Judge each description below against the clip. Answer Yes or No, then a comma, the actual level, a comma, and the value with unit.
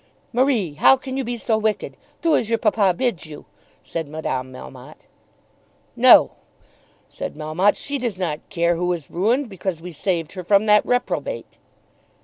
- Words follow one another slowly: No, average, 160 wpm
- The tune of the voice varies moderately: No, wide, 6.1 semitones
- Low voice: No, high, 195 Hz